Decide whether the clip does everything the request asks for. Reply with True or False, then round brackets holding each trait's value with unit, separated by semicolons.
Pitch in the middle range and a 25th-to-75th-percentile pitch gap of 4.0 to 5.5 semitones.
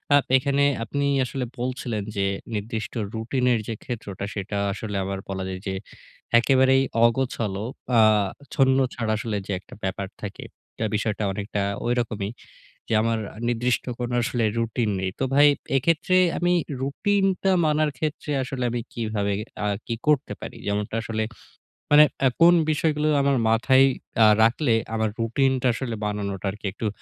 False (120 Hz; 4.3 semitones)